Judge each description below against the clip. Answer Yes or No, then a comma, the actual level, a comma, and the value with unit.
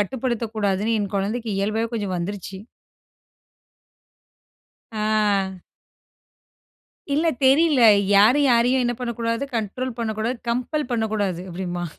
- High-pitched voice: Yes, high, 225 Hz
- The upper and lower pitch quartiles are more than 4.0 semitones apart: No, average, 3.6 semitones